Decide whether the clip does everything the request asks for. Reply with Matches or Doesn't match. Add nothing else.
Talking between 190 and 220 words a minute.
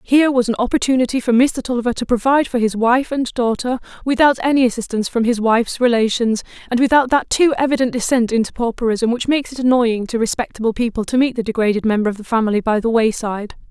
Matches